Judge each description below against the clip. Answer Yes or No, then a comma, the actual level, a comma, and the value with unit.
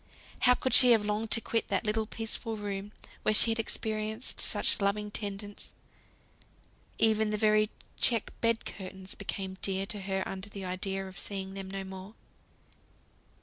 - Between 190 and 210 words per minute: No, average, 160 wpm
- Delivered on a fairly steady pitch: Yes, narrow, 2.1 semitones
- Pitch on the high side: Yes, high, 205 Hz